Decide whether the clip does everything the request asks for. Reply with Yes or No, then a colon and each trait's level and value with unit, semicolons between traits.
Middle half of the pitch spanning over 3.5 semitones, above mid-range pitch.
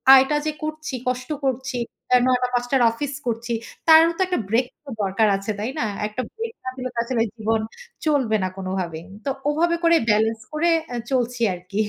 Yes: average, 4.9 semitones; very high, 250 Hz